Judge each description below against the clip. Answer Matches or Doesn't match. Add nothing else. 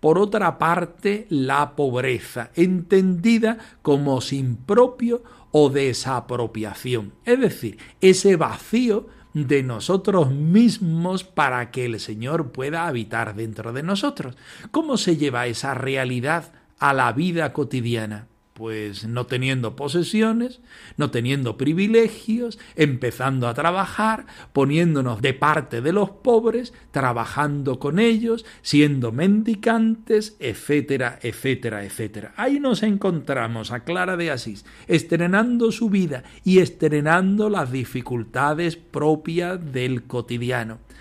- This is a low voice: Doesn't match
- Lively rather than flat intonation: Matches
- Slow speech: Matches